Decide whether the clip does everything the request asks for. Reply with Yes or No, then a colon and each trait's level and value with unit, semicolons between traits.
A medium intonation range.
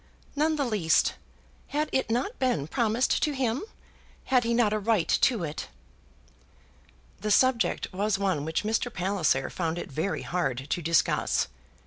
No: wide, 6.3 semitones